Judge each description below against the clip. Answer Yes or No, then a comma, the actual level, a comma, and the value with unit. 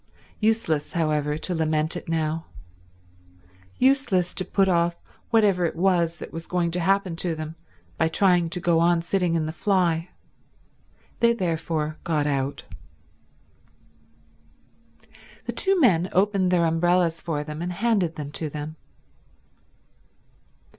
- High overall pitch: No, medium, 170 Hz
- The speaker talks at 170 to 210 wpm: No, slow, 135 wpm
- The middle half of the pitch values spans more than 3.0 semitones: No, narrow, 2.6 semitones